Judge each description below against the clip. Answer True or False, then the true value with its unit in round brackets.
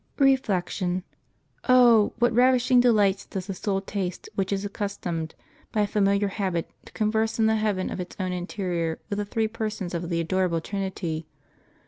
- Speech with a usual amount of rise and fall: True (3.3 semitones)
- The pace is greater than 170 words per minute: True (180 wpm)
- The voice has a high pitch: True (200 Hz)